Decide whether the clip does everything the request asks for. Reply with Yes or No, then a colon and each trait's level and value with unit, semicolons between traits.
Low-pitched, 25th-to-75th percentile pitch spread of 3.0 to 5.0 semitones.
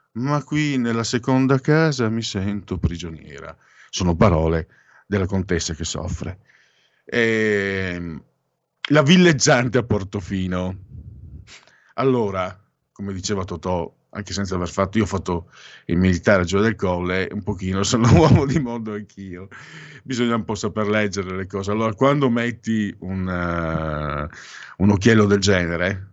Yes: low, 100 Hz; average, 4.1 semitones